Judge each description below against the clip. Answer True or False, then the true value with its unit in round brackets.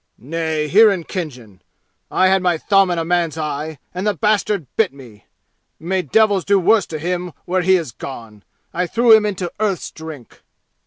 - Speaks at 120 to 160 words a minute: False (180 wpm)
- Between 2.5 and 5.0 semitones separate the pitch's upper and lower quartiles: True (4.1 semitones)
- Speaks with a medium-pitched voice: True (175 Hz)